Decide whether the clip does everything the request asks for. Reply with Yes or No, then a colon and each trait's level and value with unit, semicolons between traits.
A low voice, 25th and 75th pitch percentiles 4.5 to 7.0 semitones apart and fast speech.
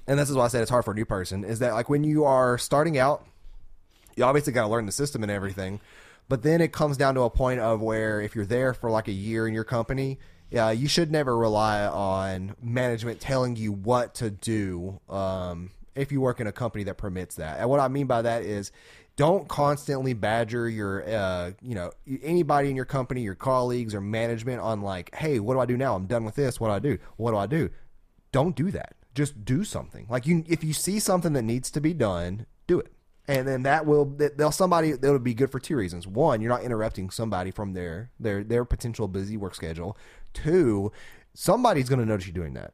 Yes: low, 115 Hz; average, 4.9 semitones; fast, 230 wpm